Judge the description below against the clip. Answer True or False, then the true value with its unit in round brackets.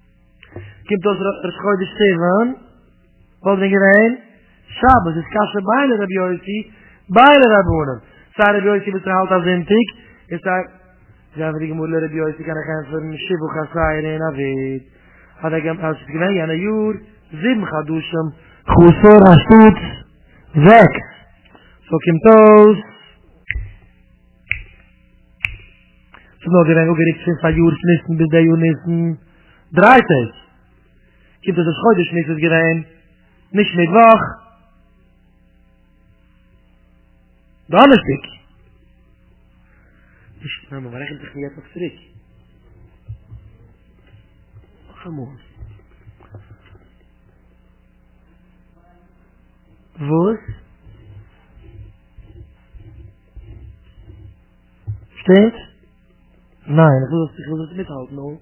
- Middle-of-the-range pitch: True (160 Hz)